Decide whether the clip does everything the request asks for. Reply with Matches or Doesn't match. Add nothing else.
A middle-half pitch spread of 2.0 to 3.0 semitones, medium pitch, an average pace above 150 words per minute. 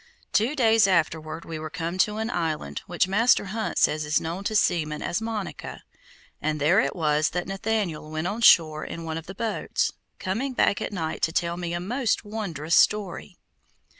Doesn't match